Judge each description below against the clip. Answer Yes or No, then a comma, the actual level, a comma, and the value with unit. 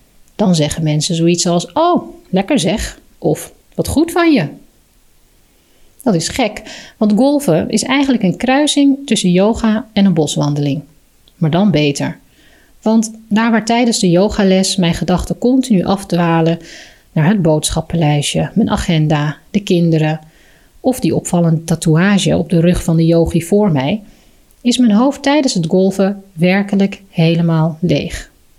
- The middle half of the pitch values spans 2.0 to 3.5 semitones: No, average, 5.0 semitones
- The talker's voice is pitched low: No, medium, 185 Hz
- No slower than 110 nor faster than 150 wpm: Yes, average, 145 wpm